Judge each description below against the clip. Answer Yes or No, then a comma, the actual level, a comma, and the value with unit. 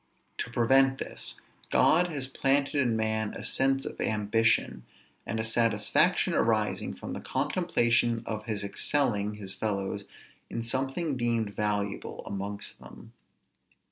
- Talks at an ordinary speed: No, slow, 130 wpm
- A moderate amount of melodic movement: Yes, average, 4.1 semitones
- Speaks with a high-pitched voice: No, low, 115 Hz